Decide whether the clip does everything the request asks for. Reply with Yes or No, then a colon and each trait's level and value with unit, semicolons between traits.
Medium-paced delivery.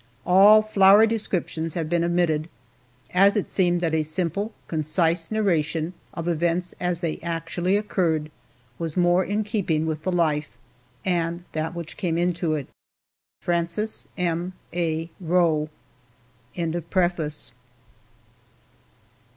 No: slow, 115 wpm